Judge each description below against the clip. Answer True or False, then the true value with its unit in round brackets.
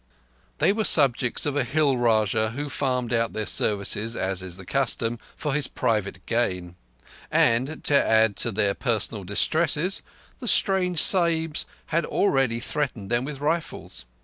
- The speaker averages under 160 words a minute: True (150 wpm)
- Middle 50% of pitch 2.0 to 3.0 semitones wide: False (5.5 semitones)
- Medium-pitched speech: False (125 Hz)